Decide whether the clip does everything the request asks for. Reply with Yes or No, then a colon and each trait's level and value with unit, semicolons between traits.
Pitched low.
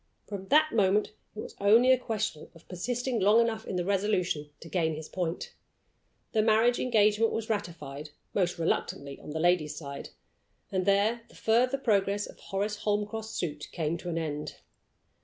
No: high, 200 Hz